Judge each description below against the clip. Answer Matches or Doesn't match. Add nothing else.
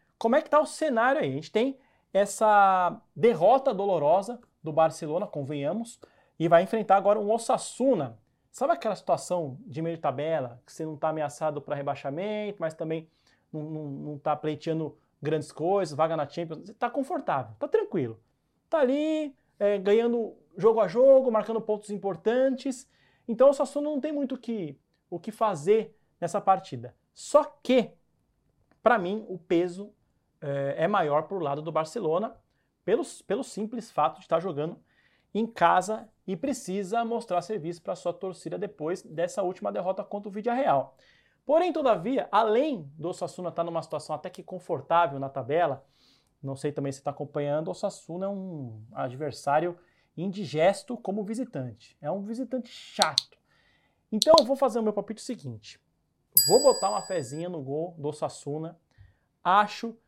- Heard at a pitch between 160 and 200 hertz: Matches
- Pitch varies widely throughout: Matches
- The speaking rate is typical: Matches